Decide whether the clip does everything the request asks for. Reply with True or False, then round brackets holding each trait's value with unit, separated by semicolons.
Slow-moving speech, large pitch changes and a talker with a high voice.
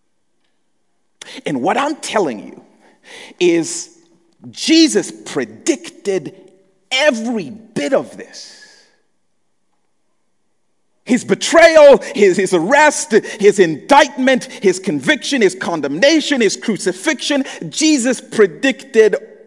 True (85 wpm; 7.2 semitones; 280 Hz)